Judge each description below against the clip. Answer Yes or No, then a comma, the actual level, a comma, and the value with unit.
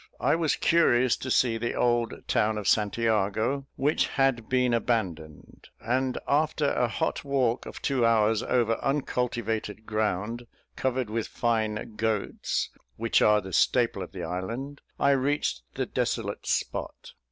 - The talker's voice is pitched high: No, low, 115 Hz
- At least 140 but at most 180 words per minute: Yes, average, 145 wpm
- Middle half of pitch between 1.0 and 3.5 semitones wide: Yes, average, 3.2 semitones